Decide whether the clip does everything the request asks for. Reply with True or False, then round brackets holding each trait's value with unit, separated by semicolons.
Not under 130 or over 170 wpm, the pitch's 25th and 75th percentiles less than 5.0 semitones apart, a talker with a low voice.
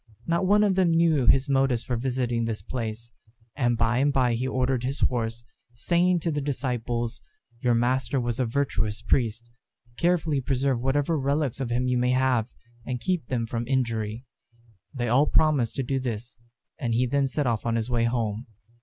False (185 wpm; 2.9 semitones; 125 Hz)